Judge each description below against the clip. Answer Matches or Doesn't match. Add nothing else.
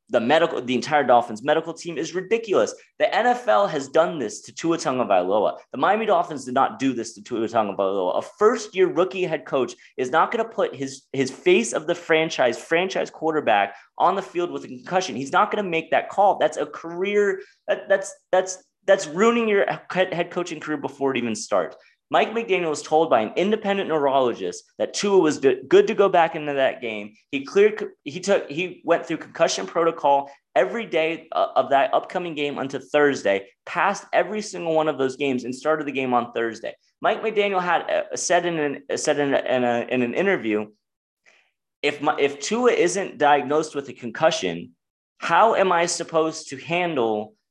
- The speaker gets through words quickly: Doesn't match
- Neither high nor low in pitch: Matches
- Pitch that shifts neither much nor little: Doesn't match